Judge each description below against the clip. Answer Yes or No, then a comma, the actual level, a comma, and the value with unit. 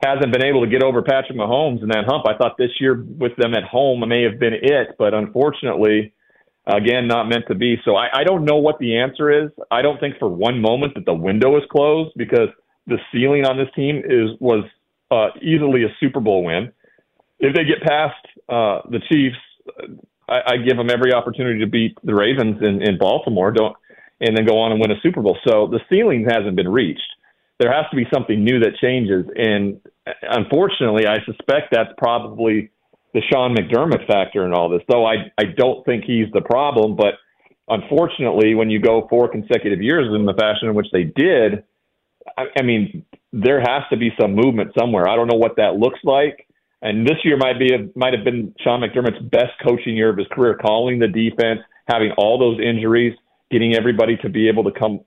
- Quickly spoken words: Yes, fast, 210 wpm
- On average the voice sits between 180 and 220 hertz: No, low, 120 Hz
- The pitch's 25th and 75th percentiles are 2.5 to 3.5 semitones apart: Yes, average, 3.1 semitones